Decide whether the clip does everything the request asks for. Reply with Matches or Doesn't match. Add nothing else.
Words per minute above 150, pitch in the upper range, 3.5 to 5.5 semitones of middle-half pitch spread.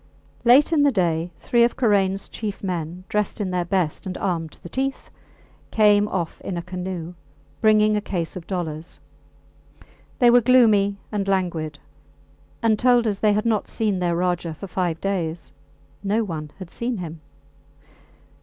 Matches